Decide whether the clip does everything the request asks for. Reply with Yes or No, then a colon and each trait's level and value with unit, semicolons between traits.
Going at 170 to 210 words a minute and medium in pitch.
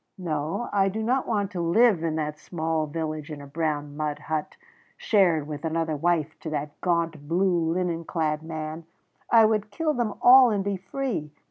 Yes: average, 180 wpm; medium, 165 Hz